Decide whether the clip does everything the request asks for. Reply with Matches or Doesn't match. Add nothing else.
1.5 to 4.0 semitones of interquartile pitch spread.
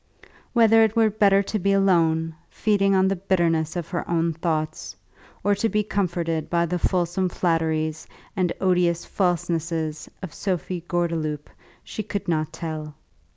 Matches